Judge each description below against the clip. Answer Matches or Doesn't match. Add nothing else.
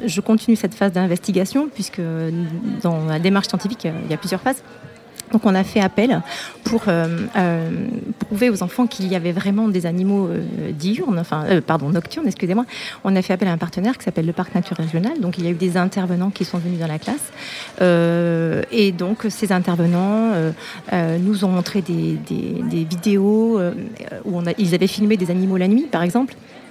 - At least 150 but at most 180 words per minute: Doesn't match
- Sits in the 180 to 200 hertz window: Matches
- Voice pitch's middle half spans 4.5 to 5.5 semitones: Doesn't match